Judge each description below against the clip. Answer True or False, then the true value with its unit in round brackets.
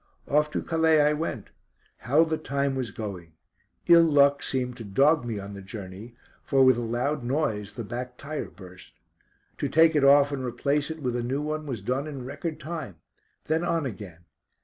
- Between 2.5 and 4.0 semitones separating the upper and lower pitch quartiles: False (4.6 semitones)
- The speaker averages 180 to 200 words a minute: True (195 wpm)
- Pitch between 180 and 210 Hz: False (135 Hz)